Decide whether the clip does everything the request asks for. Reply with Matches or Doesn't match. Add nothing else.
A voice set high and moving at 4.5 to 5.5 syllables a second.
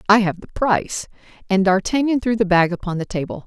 Doesn't match